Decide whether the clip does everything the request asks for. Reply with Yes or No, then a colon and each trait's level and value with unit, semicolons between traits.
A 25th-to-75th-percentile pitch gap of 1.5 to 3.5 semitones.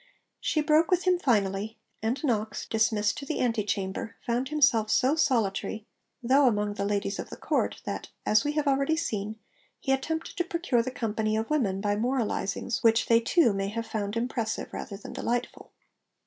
No: average, 4.5 semitones